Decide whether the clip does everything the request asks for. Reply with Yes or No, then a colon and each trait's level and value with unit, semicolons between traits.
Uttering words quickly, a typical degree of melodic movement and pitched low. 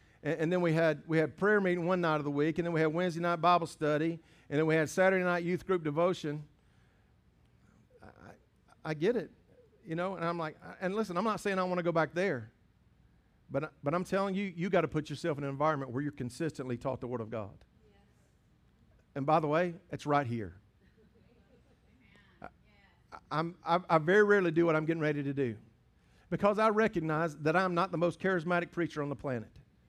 No: fast, 210 wpm; average, 3.7 semitones; medium, 160 Hz